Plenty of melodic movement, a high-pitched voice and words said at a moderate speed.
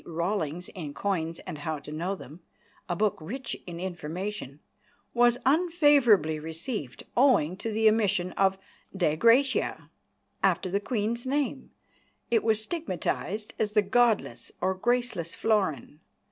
No: wide, 5.9 semitones; high, 200 Hz; slow, 130 wpm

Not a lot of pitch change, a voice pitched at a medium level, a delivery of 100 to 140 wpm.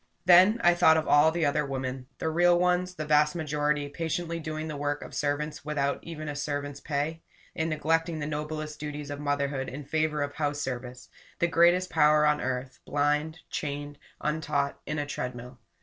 No: narrow, 1.8 semitones; medium, 150 Hz; average, 180 wpm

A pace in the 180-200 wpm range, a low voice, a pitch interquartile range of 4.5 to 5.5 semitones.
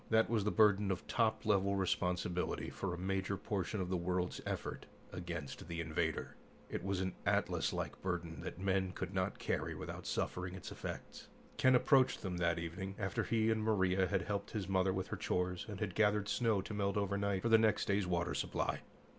No: average, 195 wpm; very low, 95 Hz; narrow, 2.4 semitones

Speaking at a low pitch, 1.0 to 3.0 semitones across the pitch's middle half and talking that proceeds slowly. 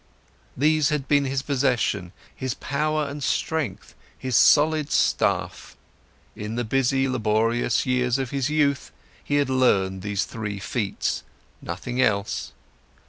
No: low, 130 Hz; average, 4.3 semitones; slow, 130 wpm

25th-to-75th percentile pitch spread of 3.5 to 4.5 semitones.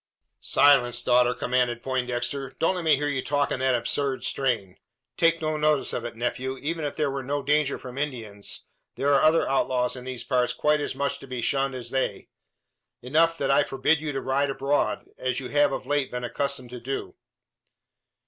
No: narrow, 2.6 semitones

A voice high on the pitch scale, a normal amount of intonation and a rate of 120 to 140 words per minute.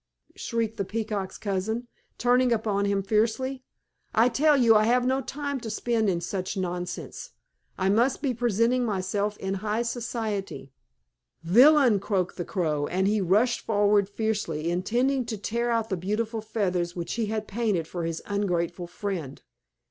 No: high, 210 Hz; average, 3.8 semitones; average, 155 wpm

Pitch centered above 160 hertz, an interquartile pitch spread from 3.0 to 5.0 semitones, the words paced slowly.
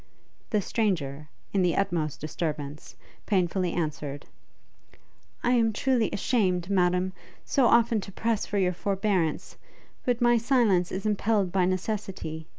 Yes: high, 190 Hz; average, 4.2 semitones; slow, 130 wpm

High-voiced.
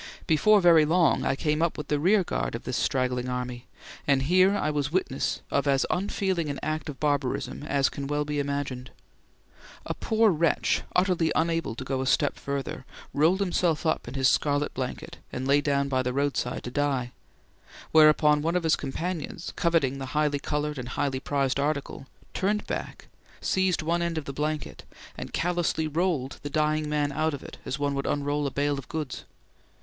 No: medium, 145 Hz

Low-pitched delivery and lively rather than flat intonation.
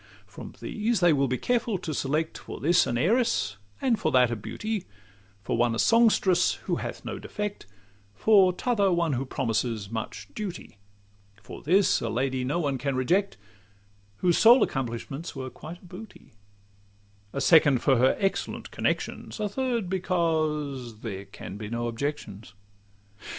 No: medium, 150 Hz; wide, 8.0 semitones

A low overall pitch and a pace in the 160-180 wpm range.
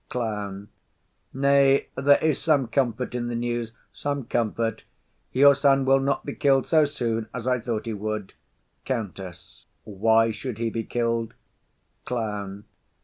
No: low, 120 Hz; average, 145 wpm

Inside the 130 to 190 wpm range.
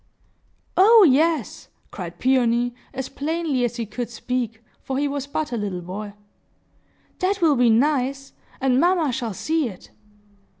Yes: average, 145 wpm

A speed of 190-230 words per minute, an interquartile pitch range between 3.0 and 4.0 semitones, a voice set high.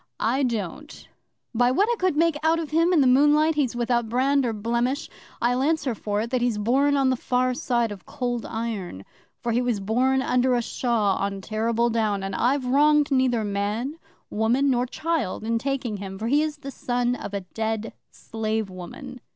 Yes: average, 195 wpm; average, 3.7 semitones; high, 245 Hz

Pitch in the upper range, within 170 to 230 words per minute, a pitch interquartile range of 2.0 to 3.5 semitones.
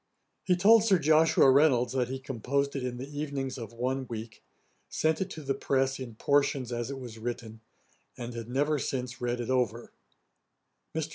No: low, 130 Hz; average, 185 wpm; average, 3.0 semitones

